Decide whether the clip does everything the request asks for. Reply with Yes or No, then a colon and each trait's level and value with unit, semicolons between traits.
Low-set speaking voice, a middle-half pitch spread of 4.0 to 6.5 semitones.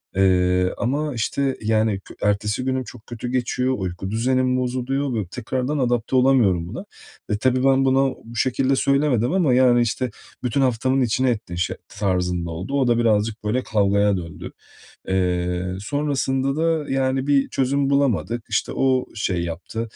Yes: low, 120 Hz; average, 4.5 semitones